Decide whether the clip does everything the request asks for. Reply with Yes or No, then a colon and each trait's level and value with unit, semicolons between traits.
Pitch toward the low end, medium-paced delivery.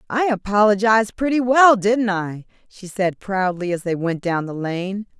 No: high, 205 Hz; average, 175 wpm